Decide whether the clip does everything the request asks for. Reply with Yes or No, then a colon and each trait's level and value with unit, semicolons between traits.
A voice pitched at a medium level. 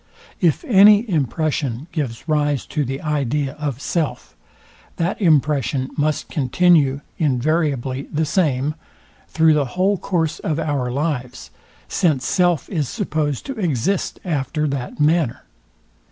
Yes: medium, 150 Hz